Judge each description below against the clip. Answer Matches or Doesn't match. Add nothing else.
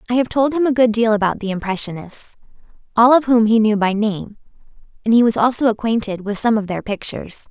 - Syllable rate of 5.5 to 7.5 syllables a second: Matches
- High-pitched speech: Matches